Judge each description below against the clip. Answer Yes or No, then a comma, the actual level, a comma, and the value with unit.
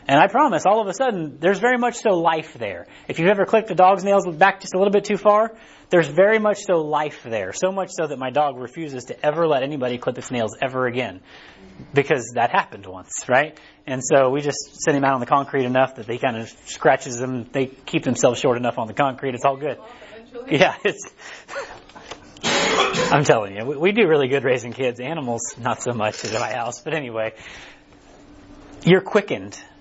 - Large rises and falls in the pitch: Yes, wide, 6.6 semitones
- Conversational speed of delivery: No, fast, 210 wpm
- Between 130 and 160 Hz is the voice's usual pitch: Yes, medium, 145 Hz